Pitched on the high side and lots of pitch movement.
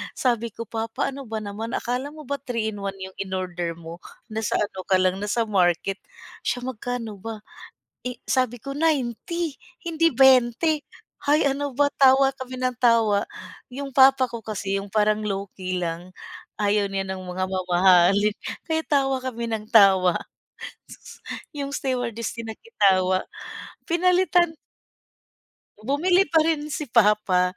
Yes: high, 230 Hz; wide, 5.7 semitones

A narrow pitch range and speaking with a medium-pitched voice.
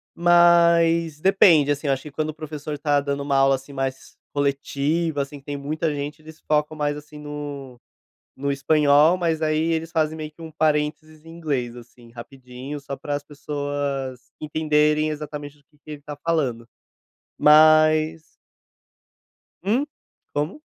Yes: narrow, 1.8 semitones; medium, 150 Hz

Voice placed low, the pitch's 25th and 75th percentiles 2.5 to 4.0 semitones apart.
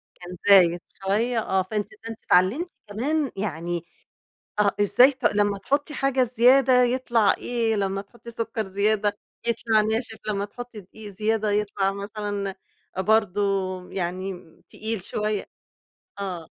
No: high, 210 Hz; average, 2.9 semitones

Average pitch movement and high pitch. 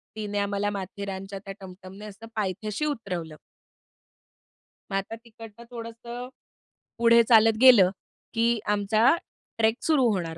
Yes: average, 3.0 semitones; high, 215 Hz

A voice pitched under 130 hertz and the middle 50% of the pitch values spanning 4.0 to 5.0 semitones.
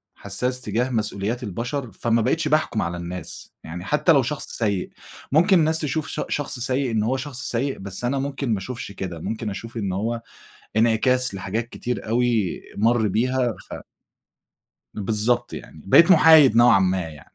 Yes: low, 115 Hz; average, 4.4 semitones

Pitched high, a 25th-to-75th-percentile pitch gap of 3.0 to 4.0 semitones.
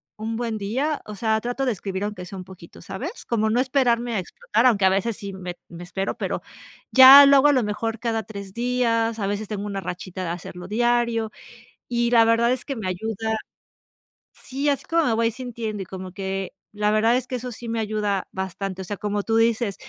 Yes: high, 220 Hz; average, 3.4 semitones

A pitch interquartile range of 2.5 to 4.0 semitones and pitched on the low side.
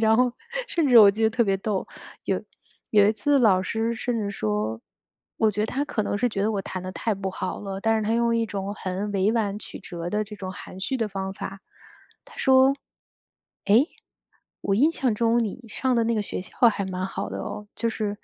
No: average, 2.9 semitones; high, 210 Hz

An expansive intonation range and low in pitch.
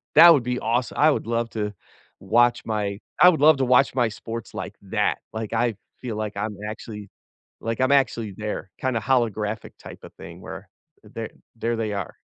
No: average, 2.8 semitones; low, 115 Hz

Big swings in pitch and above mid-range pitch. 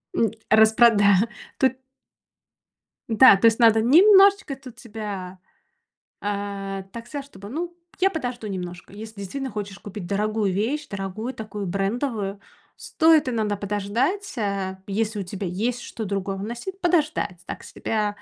No: average, 4.4 semitones; high, 220 Hz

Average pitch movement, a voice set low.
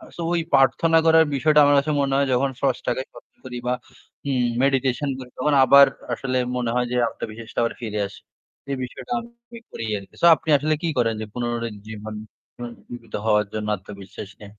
Yes: average, 3.9 semitones; low, 125 Hz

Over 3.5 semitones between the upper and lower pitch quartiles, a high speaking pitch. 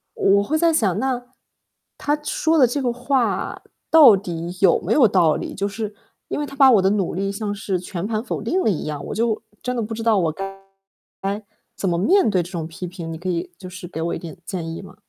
Yes: average, 5.1 semitones; high, 200 Hz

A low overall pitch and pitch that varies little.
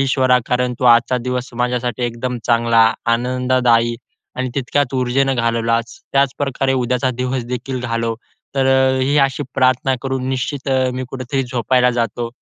Yes: low, 125 Hz; narrow, 1.6 semitones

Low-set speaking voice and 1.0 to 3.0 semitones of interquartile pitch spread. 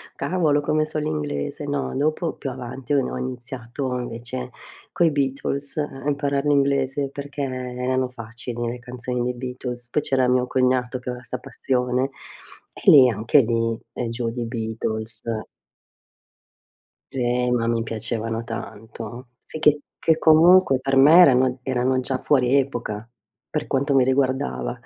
Yes: low, 130 Hz; narrow, 2.6 semitones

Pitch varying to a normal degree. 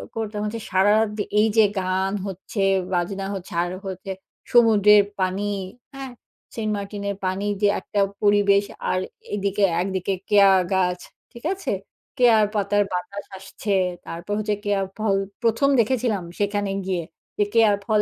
No: narrow, 1.9 semitones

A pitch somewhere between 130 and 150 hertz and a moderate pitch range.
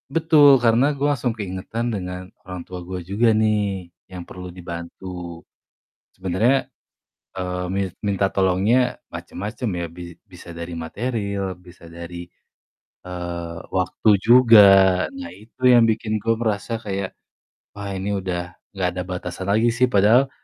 No: very low, 95 Hz; average, 3.8 semitones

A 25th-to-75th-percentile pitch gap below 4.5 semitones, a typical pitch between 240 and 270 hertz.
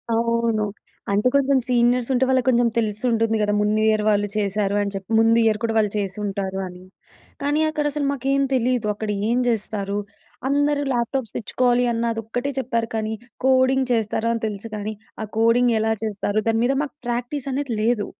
No: average, 2.9 semitones; high, 230 Hz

